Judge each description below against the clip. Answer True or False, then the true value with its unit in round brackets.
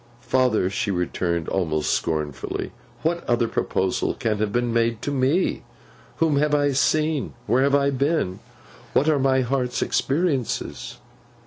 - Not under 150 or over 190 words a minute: False (140 wpm)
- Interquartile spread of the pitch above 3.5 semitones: True (5.4 semitones)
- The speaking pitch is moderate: False (130 Hz)